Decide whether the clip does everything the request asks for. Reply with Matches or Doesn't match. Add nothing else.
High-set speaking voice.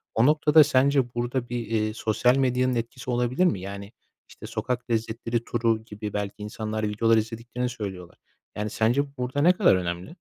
Doesn't match